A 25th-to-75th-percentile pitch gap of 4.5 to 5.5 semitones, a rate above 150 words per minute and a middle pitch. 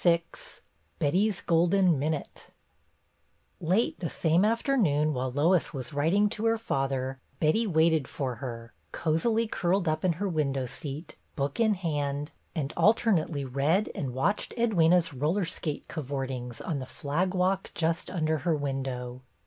No: average, 5.1 semitones; average, 145 wpm; medium, 160 Hz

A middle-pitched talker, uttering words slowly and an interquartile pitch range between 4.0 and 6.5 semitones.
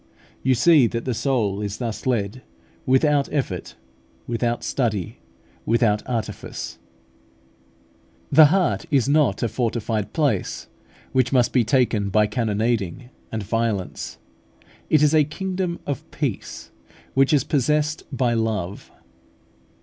No: low, 120 Hz; slow, 120 wpm; average, 4.5 semitones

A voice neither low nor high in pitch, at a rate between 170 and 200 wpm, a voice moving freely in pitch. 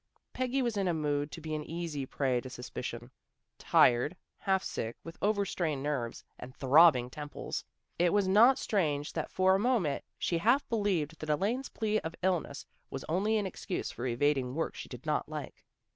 Yes: medium, 165 Hz; average, 185 wpm; wide, 6.0 semitones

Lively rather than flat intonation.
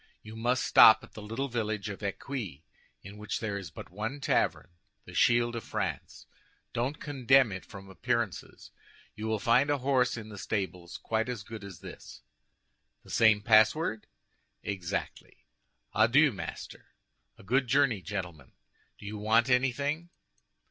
No: average, 3.9 semitones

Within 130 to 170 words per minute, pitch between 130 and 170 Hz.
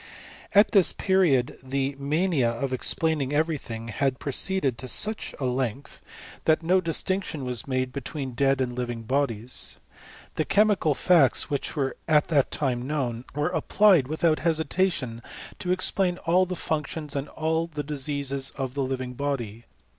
Yes: average, 160 wpm; medium, 140 Hz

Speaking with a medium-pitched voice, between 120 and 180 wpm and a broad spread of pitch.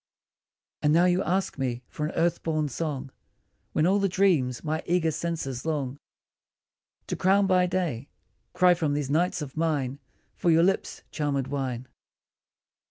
No: medium, 155 Hz; average, 155 wpm; average, 4.3 semitones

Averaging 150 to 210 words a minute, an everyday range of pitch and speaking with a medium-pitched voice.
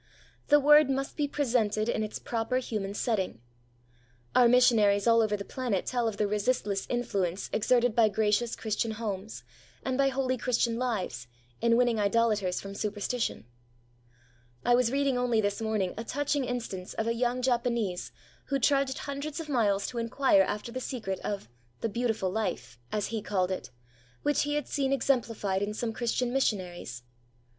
No: average, 165 wpm; average, 3.6 semitones; high, 230 Hz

